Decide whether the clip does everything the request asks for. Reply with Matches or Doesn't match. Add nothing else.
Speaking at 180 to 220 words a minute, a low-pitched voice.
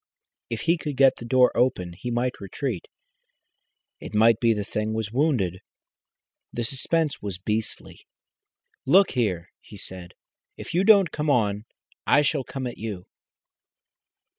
Doesn't match